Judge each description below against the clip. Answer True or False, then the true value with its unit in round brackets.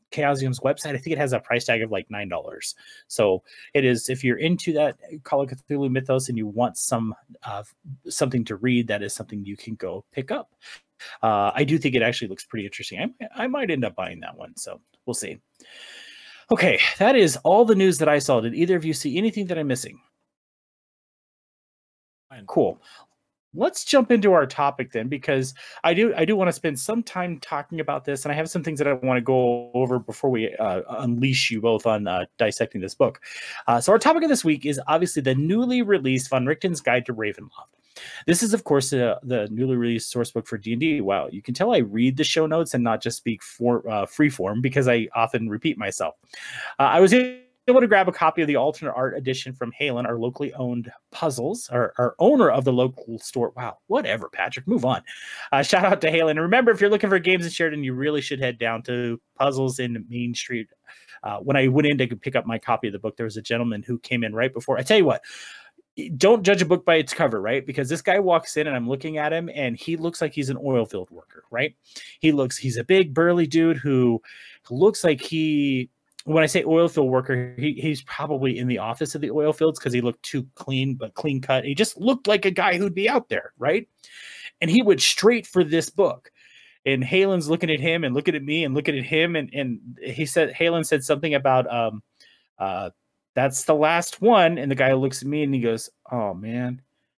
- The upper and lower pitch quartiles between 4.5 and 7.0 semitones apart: True (5.1 semitones)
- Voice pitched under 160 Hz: True (140 Hz)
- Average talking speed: False (230 wpm)